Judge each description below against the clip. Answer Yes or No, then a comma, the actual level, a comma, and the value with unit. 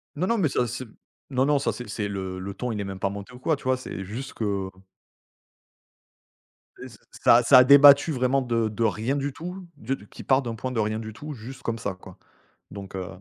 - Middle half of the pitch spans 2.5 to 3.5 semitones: No, average, 4.6 semitones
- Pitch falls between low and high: No, low, 120 Hz